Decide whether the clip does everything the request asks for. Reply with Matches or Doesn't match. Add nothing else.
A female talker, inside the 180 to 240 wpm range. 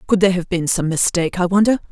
Doesn't match